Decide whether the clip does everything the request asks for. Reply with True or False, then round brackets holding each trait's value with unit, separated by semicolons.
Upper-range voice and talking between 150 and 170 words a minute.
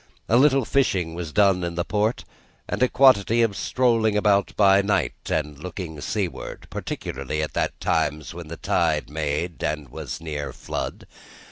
False (90 Hz; 160 wpm)